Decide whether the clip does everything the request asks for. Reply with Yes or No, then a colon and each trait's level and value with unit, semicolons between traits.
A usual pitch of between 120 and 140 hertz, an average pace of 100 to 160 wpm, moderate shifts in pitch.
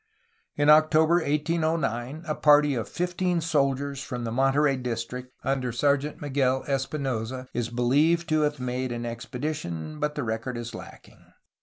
Yes: low, 135 Hz; average, 150 wpm; average, 3.6 semitones